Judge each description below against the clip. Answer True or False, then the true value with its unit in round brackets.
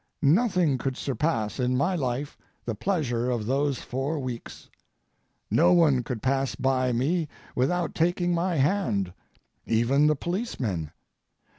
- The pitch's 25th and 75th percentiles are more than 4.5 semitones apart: True (5.3 semitones)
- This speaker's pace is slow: True (130 wpm)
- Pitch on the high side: False (135 Hz)